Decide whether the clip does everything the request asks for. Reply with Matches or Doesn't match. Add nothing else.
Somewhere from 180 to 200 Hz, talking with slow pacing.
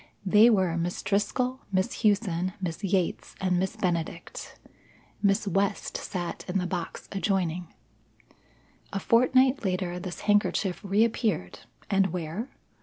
Matches